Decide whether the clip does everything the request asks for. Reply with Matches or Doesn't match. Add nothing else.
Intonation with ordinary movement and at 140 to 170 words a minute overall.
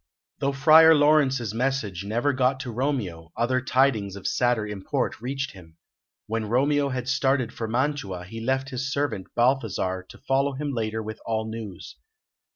Matches